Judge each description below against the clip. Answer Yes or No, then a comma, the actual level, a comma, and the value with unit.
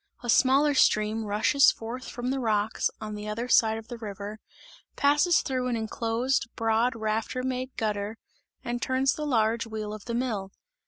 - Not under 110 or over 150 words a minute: No, average, 170 wpm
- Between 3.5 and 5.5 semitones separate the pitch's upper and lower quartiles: No, average, 2.9 semitones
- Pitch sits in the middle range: No, high, 230 Hz